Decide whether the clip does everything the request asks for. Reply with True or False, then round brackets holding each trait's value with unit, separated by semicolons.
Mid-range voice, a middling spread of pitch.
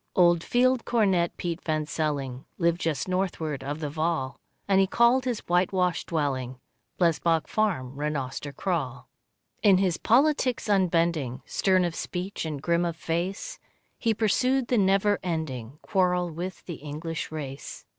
True (170 Hz; 4.2 semitones)